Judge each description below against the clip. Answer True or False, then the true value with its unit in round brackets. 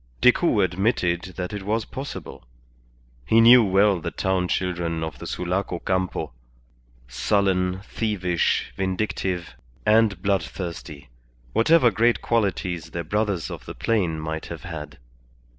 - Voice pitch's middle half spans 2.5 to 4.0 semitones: True (3.6 semitones)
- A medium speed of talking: False (125 wpm)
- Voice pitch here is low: True (95 Hz)